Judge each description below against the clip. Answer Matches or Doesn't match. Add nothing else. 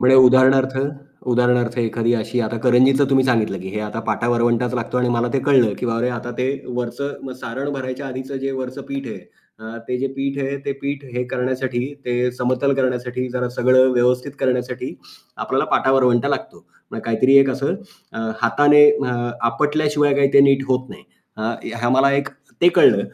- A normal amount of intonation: Doesn't match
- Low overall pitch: Matches